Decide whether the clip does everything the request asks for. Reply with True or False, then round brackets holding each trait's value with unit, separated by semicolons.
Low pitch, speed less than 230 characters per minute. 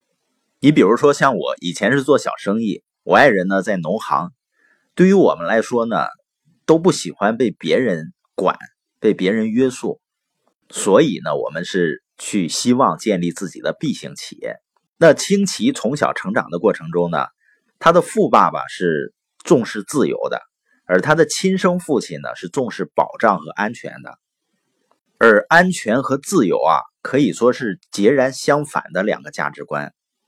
False (130 Hz; 235 characters per minute)